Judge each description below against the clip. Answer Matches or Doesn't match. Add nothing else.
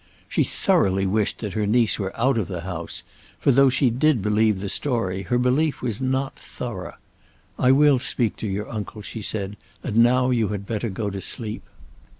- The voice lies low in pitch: Matches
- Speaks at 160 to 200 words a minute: Matches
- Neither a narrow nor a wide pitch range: Matches